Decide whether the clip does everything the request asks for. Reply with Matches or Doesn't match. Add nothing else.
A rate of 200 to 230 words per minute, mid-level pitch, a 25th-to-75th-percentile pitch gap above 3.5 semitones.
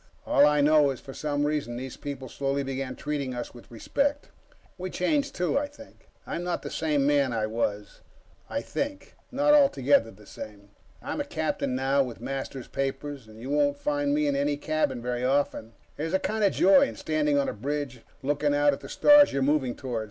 Doesn't match